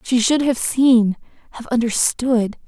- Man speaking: No, female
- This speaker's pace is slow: Yes, slow, 110 wpm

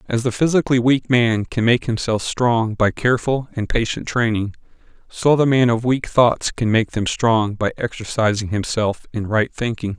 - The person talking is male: Yes, male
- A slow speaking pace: No, average, 180 wpm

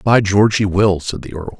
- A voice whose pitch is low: Yes, low, 100 Hz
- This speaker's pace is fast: Yes, fast, 265 wpm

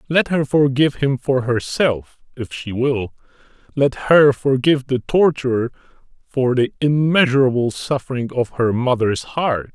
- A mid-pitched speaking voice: No, low, 130 Hz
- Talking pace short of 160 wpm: Yes, slow, 135 wpm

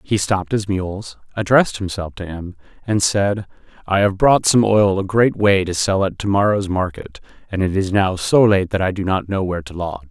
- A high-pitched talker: No, very low, 95 Hz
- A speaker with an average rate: No, fast, 225 wpm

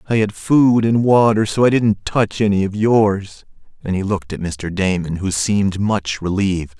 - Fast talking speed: No, average, 195 wpm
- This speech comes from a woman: No, male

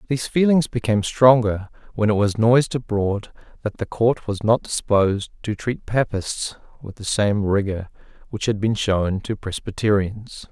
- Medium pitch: No, low, 110 Hz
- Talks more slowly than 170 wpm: Yes, average, 160 wpm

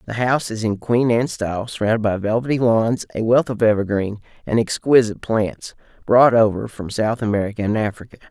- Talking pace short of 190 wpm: Yes, average, 180 wpm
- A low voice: Yes, low, 110 Hz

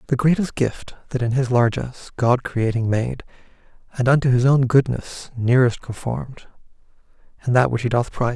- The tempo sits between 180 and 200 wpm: No, average, 165 wpm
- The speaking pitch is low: Yes, low, 125 Hz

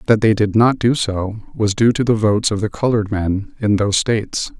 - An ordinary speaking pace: No, fast, 235 wpm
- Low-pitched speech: Yes, low, 105 Hz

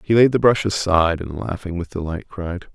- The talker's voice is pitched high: No, very low, 95 Hz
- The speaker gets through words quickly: Yes, fast, 220 wpm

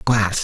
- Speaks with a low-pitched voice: Yes, low, 105 Hz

